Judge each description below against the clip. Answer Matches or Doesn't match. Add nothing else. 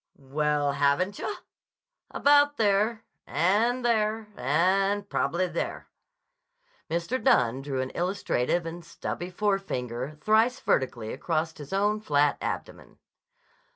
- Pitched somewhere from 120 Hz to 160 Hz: Doesn't match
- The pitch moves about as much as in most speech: Doesn't match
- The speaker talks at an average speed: Doesn't match